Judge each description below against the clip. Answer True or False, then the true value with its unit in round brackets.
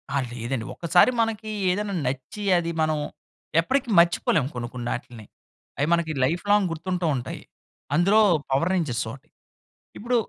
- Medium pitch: True (170 Hz)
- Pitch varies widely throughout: True (7.3 semitones)